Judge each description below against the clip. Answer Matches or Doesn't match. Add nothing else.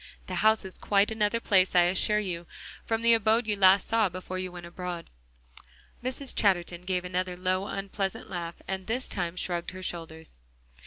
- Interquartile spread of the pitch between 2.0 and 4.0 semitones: Matches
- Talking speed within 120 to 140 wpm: Doesn't match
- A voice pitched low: Doesn't match